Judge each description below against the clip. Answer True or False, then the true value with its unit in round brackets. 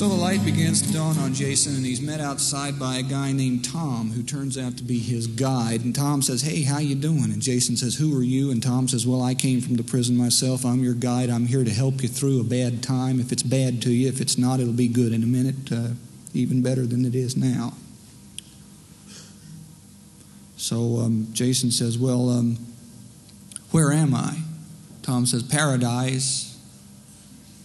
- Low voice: True (125 Hz)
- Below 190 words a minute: False (200 wpm)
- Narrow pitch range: True (2.1 semitones)